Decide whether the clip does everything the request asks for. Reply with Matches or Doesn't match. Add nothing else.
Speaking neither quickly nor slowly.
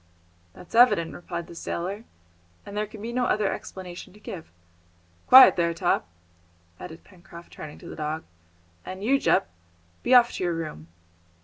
Matches